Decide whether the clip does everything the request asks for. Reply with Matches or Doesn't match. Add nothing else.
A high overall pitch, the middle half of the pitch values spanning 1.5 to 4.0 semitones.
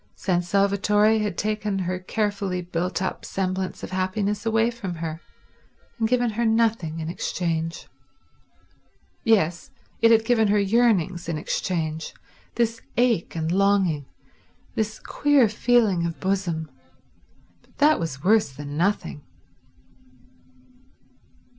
Doesn't match